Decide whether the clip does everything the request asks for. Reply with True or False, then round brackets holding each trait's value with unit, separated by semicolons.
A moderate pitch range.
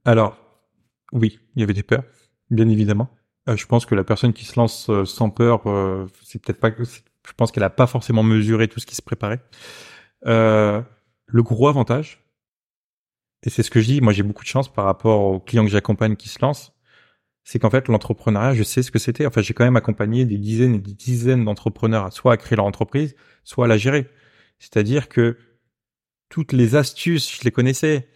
False (2.3 semitones)